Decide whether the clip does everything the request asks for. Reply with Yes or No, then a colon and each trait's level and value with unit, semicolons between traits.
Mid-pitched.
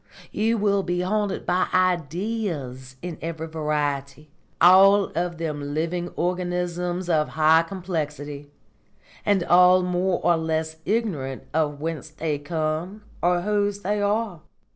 Yes: medium, 175 Hz